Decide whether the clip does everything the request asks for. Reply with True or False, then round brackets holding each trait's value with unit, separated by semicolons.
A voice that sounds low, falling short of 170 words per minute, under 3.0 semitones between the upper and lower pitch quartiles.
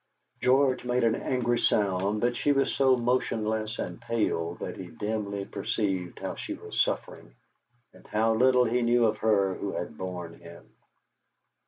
False (110 Hz; 160 wpm; 4.0 semitones)